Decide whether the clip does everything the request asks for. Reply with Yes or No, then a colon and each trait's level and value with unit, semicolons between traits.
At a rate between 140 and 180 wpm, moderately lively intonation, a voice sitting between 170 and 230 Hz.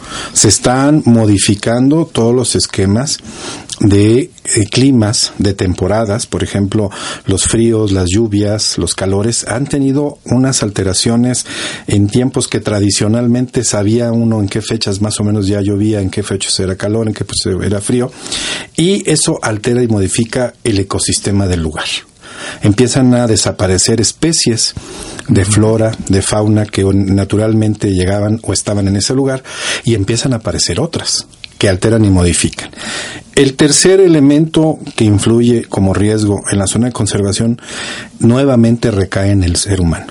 No: average, 150 wpm; average, 3.5 semitones; low, 110 Hz